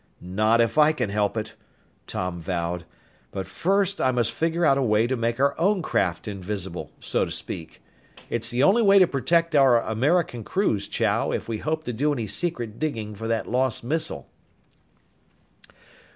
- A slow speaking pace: No, average, 175 wpm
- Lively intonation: Yes, wide, 6.6 semitones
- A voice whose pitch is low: Yes, low, 120 Hz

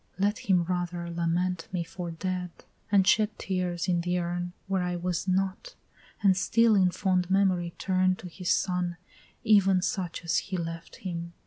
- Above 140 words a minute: Yes, average, 165 wpm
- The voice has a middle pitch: Yes, medium, 180 Hz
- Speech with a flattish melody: Yes, narrow, 1.5 semitones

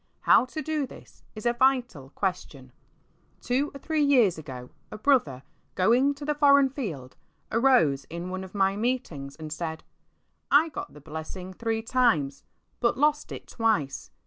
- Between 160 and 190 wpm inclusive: Yes, average, 165 wpm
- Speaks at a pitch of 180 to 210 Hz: No, high, 220 Hz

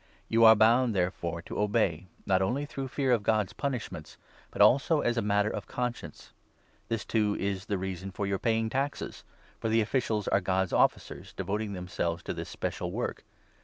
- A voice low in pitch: Yes, low, 105 Hz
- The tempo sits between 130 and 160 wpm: No, average, 200 wpm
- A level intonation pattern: No, average, 3.5 semitones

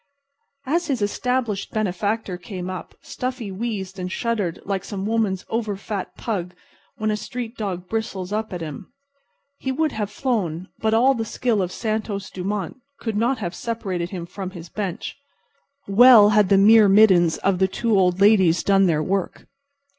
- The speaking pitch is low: No, high, 205 Hz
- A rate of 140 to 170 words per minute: Yes, average, 165 wpm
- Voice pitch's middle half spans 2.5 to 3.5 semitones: Yes, average, 3.2 semitones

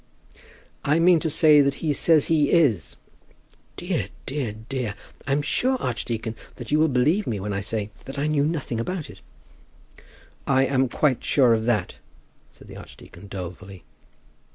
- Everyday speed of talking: Yes, average, 160 wpm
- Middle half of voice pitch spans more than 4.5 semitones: Yes, wide, 5.4 semitones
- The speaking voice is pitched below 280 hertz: Yes, low, 135 Hz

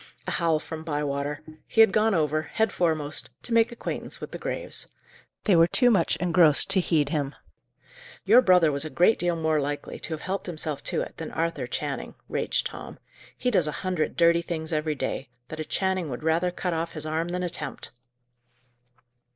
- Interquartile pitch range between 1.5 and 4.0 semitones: Yes, average, 2.8 semitones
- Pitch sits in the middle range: Yes, medium, 165 Hz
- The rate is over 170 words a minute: Yes, average, 190 wpm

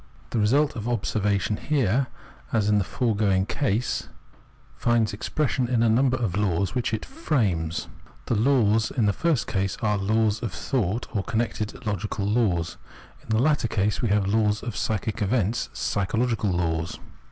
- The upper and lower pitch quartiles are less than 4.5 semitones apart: Yes, average, 3.0 semitones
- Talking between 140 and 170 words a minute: No, average, 180 wpm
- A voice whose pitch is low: Yes, low, 110 Hz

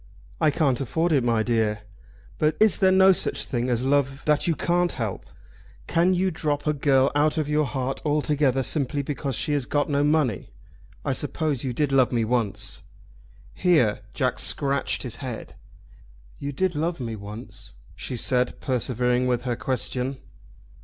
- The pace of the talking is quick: No, average, 165 wpm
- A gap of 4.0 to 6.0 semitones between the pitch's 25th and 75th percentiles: No, average, 3.6 semitones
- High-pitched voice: No, medium, 140 Hz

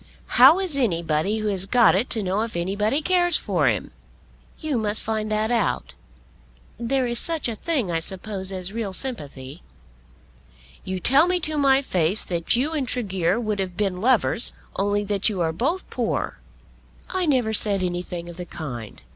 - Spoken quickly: No, average, 175 wpm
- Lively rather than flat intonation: Yes, wide, 5.8 semitones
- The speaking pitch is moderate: No, high, 215 Hz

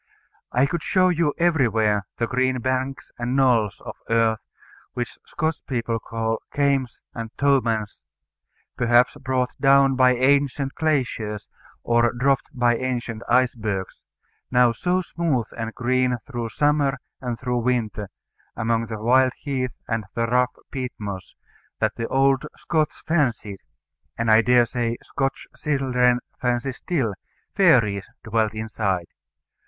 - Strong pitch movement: No, average, 3.1 semitones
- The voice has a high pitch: No, low, 125 Hz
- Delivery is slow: Yes, slow, 130 wpm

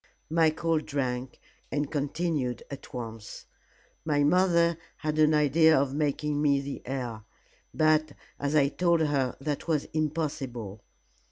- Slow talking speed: Yes, slow, 125 wpm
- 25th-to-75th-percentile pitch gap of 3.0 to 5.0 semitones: No, narrow, 2.5 semitones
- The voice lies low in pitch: No, medium, 145 Hz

